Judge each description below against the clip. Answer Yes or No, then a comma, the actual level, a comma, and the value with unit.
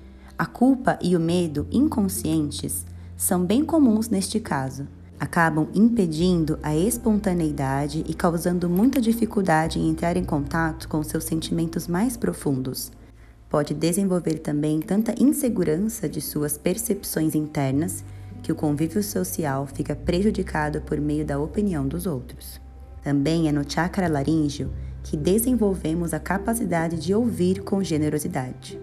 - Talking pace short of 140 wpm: Yes, average, 130 wpm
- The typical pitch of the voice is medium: Yes, medium, 160 Hz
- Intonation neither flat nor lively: Yes, average, 4.5 semitones